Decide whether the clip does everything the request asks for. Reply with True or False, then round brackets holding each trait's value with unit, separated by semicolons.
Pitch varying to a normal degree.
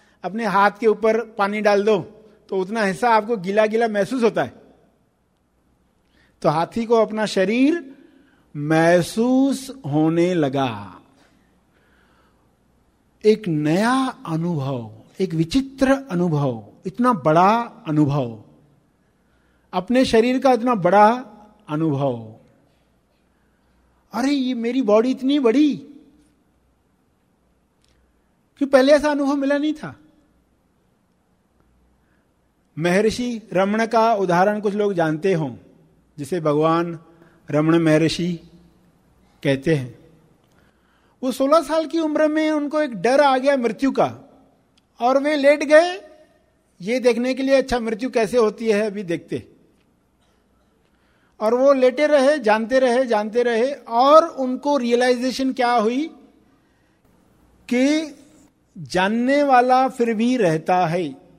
False (7.9 semitones)